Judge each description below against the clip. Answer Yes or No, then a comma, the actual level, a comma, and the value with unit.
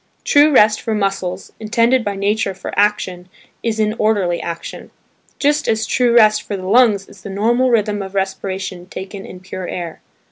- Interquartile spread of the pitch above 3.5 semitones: No, narrow, 2.6 semitones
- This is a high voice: Yes, high, 205 Hz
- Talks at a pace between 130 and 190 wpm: Yes, average, 175 wpm